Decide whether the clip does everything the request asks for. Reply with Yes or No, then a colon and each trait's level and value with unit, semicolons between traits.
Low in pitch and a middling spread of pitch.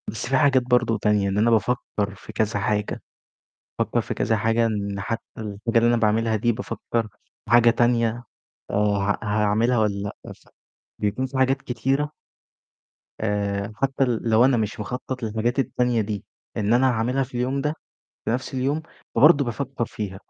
Yes: low, 115 Hz; average, 3.1 semitones